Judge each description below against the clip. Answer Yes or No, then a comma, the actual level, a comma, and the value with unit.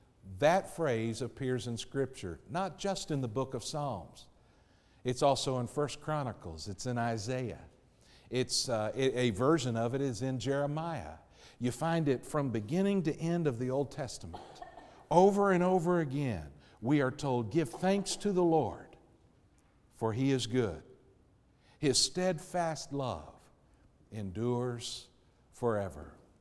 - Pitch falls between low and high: No, low, 130 Hz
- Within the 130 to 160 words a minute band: Yes, average, 140 wpm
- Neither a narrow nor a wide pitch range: Yes, average, 4.7 semitones